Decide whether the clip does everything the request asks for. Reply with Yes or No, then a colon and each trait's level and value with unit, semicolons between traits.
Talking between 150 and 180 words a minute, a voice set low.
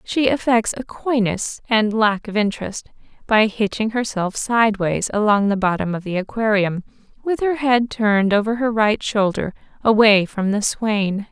No: average, 160 wpm; high, 215 Hz